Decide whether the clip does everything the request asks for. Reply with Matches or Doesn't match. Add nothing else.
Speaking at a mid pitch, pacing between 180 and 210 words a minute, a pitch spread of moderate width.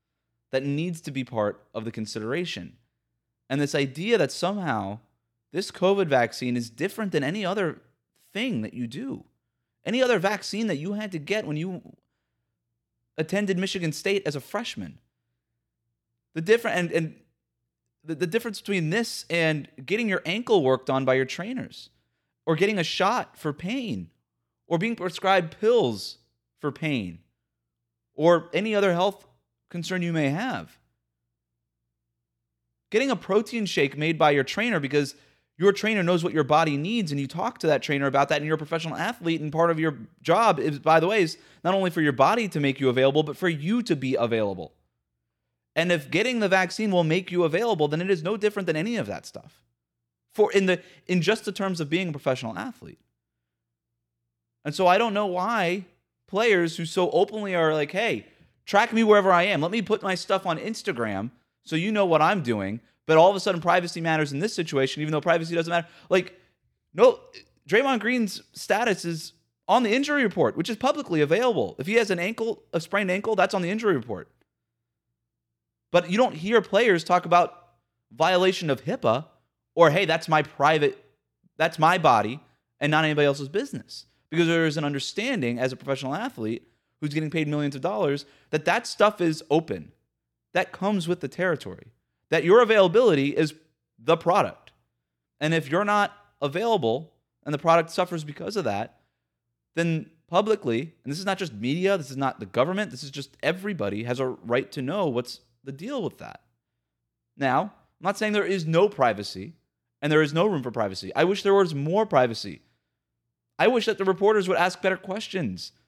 Doesn't match